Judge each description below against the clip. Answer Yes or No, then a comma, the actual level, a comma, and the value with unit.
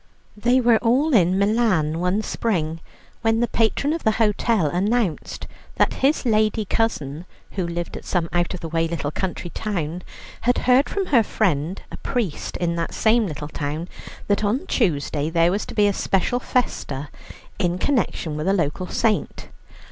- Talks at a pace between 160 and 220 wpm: Yes, average, 170 wpm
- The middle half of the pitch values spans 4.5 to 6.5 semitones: Yes, wide, 5.4 semitones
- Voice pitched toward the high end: Yes, high, 195 Hz